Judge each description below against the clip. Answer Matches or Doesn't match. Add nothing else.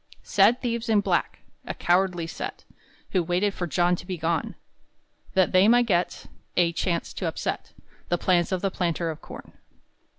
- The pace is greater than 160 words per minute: Matches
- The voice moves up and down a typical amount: Doesn't match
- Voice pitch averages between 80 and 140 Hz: Doesn't match